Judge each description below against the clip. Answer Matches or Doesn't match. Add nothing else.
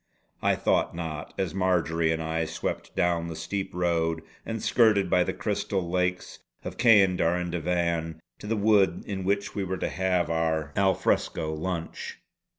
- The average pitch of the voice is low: Matches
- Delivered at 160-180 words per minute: Matches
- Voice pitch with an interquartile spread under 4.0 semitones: Matches